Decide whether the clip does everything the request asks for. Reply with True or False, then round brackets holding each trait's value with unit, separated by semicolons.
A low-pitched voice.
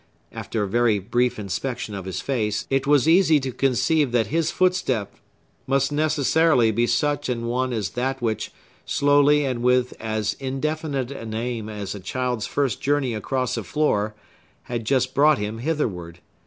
True (125 Hz)